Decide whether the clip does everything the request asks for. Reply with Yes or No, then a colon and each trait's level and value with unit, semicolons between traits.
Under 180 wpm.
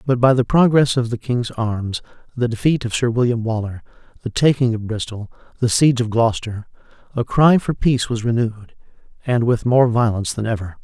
No: average, 190 wpm